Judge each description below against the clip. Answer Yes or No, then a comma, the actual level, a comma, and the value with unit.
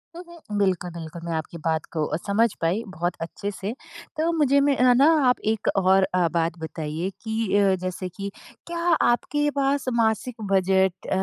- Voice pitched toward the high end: Yes, high, 195 Hz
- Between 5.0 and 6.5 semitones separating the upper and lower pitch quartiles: Yes, wide, 5.6 semitones